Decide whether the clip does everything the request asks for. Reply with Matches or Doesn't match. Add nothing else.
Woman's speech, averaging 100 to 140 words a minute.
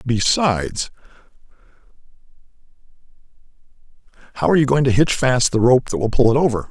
Doesn't match